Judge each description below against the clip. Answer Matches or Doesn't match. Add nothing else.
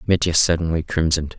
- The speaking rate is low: Matches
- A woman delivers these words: Doesn't match